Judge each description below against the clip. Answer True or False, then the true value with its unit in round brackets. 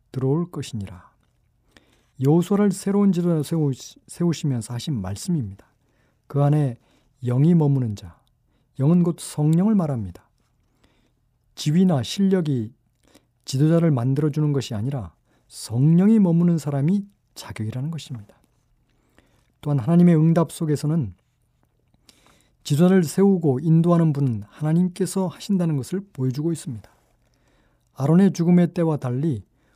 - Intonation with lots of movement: True (5.7 semitones)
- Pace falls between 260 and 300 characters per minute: True (280 characters per minute)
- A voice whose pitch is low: False (145 Hz)